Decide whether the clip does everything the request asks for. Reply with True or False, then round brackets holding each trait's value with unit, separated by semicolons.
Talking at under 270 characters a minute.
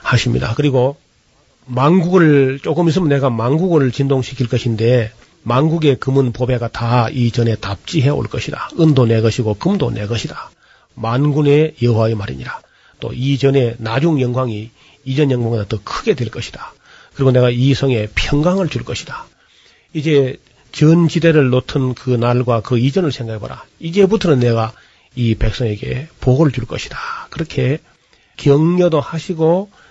False (305 characters per minute)